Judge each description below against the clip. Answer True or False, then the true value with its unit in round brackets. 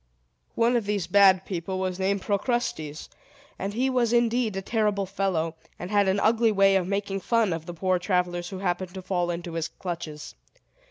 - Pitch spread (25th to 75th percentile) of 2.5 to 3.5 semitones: True (2.8 semitones)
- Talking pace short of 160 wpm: False (185 wpm)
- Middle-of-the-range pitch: False (195 Hz)